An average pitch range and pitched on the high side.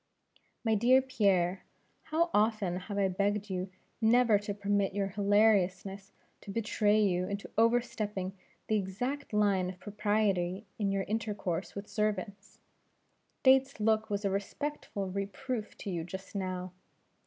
No: narrow, 2.3 semitones; high, 205 Hz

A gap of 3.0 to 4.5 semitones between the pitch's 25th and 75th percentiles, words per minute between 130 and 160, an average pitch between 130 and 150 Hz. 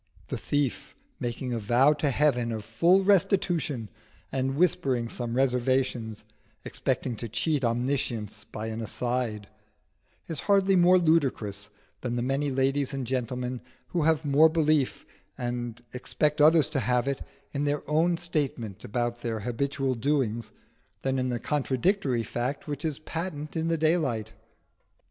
Yes: average, 4.1 semitones; average, 145 wpm; low, 135 Hz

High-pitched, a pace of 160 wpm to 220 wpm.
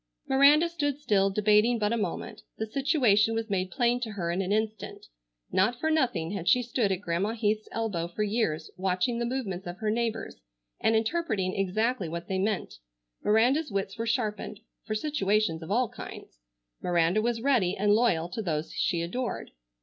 Yes: high, 215 Hz; average, 180 wpm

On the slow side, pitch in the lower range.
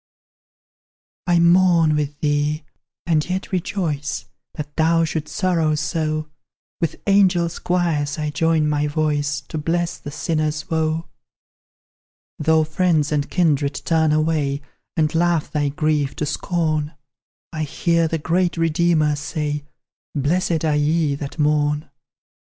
No: slow, 125 wpm; medium, 155 Hz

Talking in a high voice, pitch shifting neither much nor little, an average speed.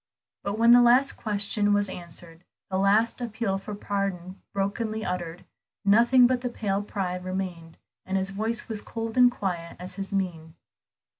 Yes: high, 200 Hz; average, 3.5 semitones; average, 160 wpm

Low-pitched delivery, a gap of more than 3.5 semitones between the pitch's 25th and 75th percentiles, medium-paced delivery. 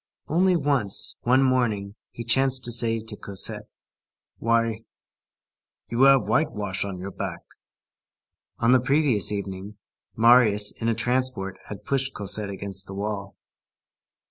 No: low, 115 Hz; average, 4.3 semitones; slow, 130 wpm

